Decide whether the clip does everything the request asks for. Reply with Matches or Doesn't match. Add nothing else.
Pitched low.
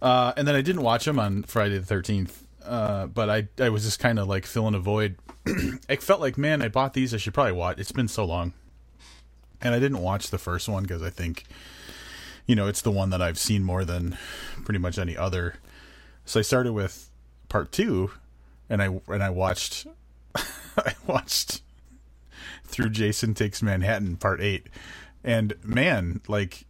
Matches